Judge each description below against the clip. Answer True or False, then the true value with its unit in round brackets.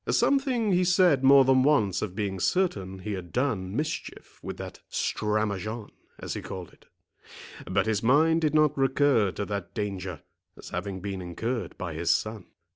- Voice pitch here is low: True (110 Hz)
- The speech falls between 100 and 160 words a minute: False (170 wpm)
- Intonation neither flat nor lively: False (6.9 semitones)